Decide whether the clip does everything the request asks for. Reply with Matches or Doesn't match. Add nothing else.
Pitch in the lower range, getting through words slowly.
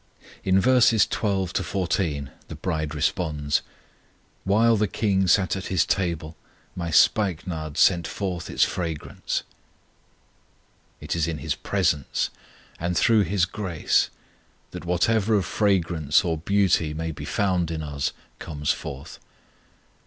Matches